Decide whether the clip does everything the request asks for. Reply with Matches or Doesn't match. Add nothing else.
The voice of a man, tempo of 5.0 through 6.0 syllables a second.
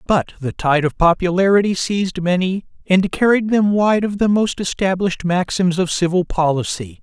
Matches